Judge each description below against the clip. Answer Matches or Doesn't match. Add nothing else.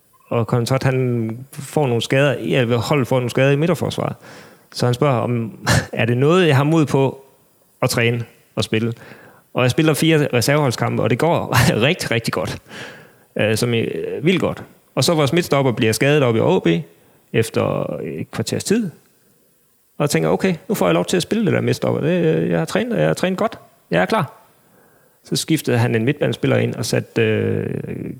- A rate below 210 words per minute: Matches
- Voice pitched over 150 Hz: Doesn't match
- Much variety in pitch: Doesn't match